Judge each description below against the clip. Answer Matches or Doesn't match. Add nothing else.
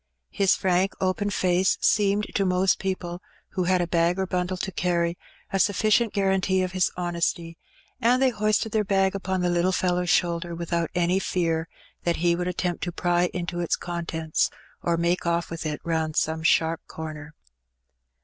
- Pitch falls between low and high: Matches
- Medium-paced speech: Matches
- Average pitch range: Doesn't match